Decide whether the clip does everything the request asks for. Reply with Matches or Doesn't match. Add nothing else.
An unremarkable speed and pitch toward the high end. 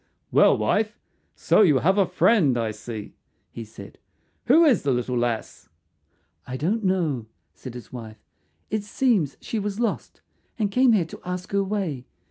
Doesn't match